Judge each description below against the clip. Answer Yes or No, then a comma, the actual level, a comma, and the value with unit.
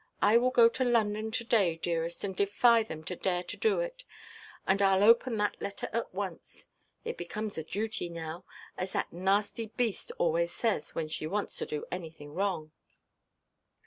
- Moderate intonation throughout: Yes, average, 4.6 semitones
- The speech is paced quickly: No, average, 175 wpm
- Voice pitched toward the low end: No, high, 200 Hz